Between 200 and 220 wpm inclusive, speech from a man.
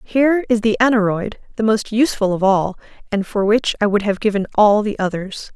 No: fast, 205 wpm; female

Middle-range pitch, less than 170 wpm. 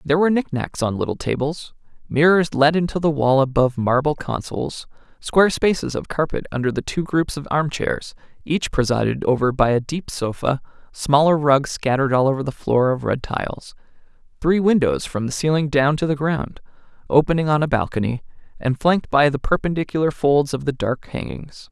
No: medium, 145 Hz; average, 180 wpm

